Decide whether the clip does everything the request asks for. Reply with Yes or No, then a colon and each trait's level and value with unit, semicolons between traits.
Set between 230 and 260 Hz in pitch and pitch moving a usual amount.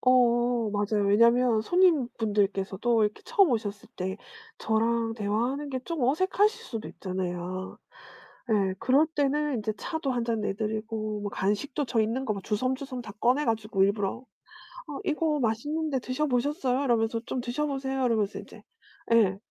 Yes: high, 235 Hz; average, 4.3 semitones